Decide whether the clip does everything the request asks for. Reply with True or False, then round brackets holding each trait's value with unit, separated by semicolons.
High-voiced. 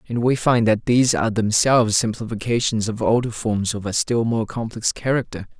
False (115 Hz)